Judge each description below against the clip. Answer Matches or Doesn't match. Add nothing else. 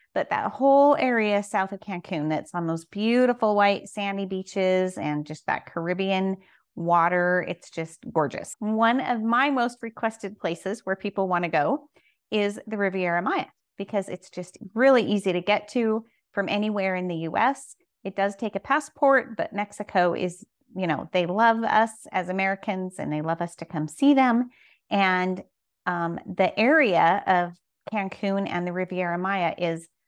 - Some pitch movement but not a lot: Matches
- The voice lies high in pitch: Matches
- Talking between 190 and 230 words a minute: Doesn't match